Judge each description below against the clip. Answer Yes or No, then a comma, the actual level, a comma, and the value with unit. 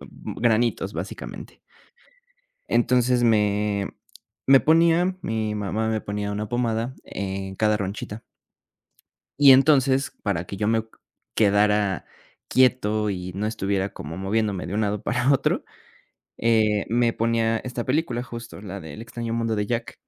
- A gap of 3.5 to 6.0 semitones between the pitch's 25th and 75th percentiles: No, average, 2.9 semitones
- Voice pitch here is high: No, low, 110 Hz